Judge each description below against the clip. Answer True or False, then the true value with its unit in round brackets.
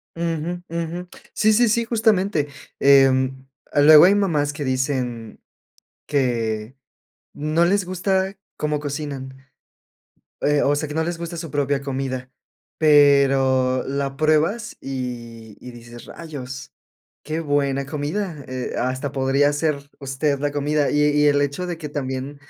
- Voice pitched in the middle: True (145 Hz)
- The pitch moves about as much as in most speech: True (3.3 semitones)